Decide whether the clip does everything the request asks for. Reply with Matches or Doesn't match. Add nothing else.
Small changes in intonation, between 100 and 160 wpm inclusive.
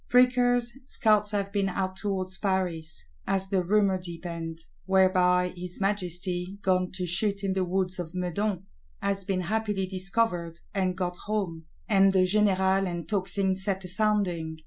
Matches